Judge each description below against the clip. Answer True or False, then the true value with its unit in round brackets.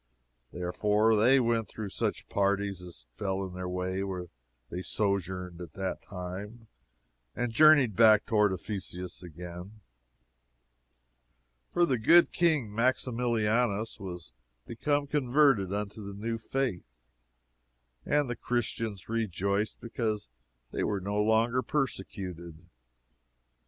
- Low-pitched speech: True (105 Hz)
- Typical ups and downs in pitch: True (4.1 semitones)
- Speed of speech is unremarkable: False (115 wpm)